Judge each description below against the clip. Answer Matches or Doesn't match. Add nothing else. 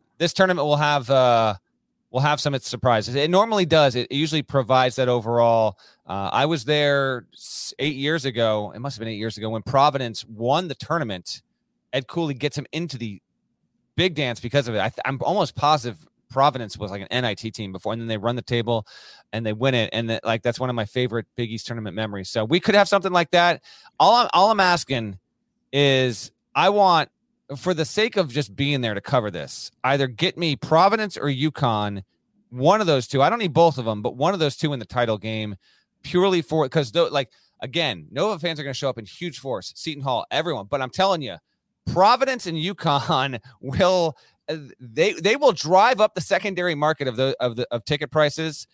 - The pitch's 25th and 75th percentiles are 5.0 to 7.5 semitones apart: Matches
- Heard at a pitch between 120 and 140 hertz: Matches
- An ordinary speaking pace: Doesn't match